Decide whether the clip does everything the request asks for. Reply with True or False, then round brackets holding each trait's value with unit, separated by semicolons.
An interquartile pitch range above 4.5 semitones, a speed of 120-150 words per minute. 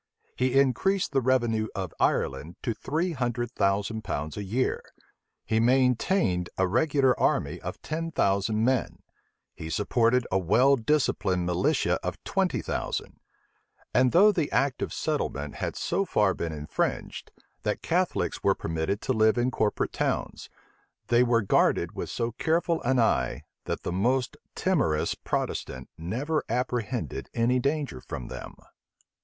True (5.4 semitones; 145 wpm)